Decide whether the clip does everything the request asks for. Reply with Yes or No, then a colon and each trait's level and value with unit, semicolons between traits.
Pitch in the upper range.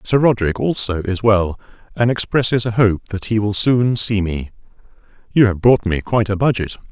No: low, 105 Hz